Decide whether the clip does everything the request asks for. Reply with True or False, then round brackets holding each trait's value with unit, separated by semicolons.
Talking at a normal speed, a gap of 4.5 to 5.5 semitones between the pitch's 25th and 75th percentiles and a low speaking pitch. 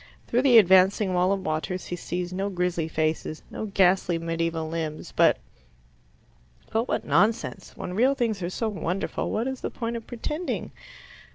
False (165 wpm; 4.9 semitones; 185 Hz)